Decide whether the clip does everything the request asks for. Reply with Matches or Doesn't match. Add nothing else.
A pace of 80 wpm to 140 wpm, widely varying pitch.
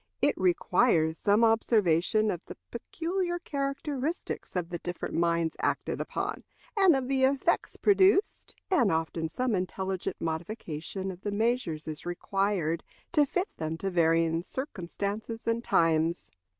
Matches